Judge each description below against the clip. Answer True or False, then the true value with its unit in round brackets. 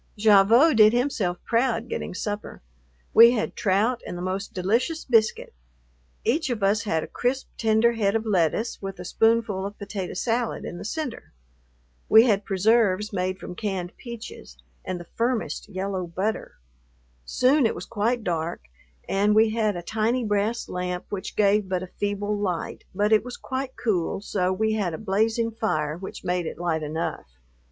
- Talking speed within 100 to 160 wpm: False (170 wpm)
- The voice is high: True (210 Hz)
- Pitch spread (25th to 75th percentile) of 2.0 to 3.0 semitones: False (3.6 semitones)